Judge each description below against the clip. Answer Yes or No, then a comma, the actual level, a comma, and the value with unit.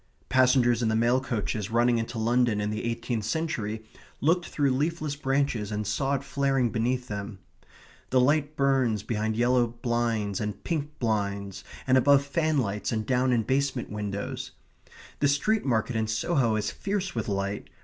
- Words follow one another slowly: No, average, 160 wpm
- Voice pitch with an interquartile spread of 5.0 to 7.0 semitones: No, average, 4.1 semitones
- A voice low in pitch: Yes, low, 120 Hz